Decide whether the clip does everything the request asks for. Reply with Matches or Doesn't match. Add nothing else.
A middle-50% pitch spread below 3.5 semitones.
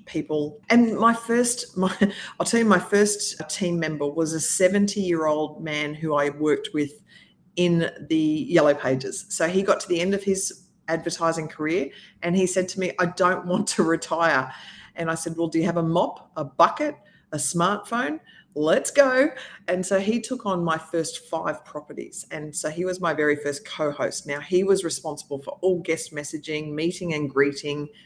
Doesn't match